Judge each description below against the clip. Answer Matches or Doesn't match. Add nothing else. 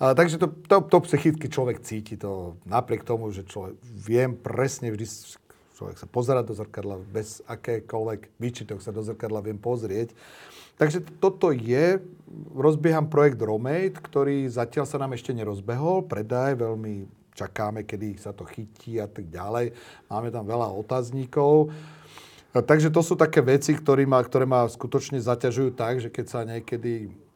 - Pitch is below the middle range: Matches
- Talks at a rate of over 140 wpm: Matches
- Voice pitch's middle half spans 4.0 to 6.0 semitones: Matches